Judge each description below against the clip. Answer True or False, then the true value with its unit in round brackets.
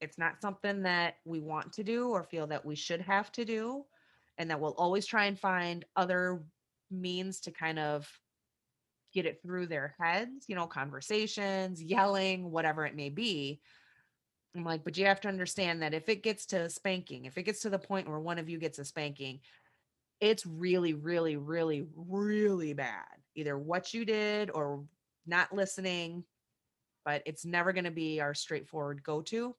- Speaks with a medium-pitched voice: True (175 Hz)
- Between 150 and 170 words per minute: False (185 wpm)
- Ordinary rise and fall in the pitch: True (4.1 semitones)